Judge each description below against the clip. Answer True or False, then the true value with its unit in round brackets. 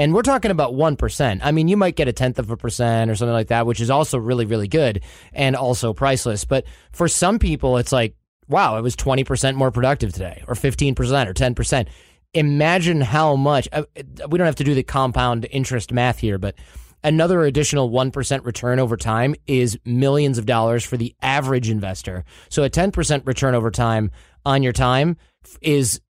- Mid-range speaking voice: False (130 Hz)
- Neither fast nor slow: True (190 wpm)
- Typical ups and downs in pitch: True (3.6 semitones)